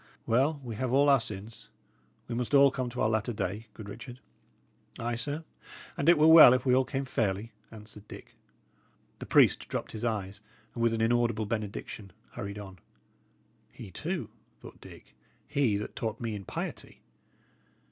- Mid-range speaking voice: No, low, 115 Hz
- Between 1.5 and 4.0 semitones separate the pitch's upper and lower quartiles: Yes, average, 3.5 semitones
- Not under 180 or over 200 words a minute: No, average, 170 wpm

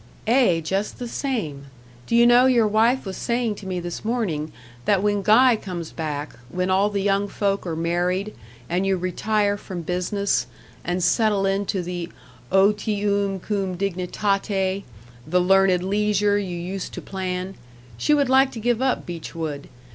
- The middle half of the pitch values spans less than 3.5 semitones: Yes, average, 2.8 semitones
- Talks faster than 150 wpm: Yes, average, 160 wpm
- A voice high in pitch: Yes, high, 195 Hz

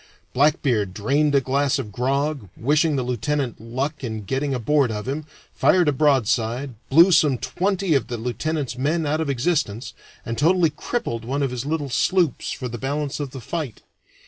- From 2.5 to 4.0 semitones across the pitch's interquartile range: Yes, average, 3.6 semitones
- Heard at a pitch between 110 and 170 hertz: Yes, medium, 140 Hz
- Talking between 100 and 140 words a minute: No, average, 175 wpm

